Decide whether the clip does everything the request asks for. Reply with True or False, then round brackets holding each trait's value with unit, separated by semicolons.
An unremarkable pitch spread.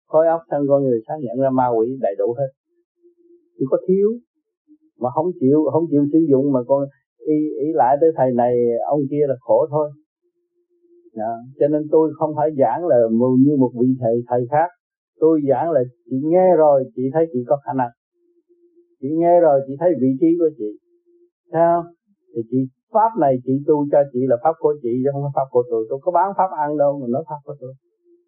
False (7.4 semitones)